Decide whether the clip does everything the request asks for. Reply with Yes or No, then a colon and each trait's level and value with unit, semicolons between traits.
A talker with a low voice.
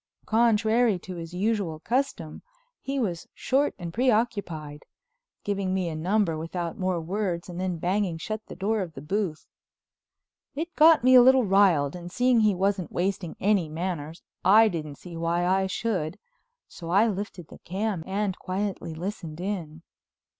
No: high, 190 Hz